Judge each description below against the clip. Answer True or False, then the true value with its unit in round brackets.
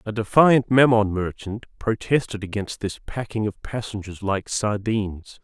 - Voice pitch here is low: True (105 Hz)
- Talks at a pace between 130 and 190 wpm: True (135 wpm)